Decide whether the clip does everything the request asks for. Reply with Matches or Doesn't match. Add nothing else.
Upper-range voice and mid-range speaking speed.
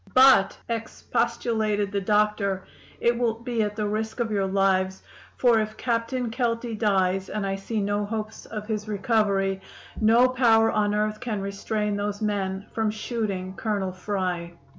Matches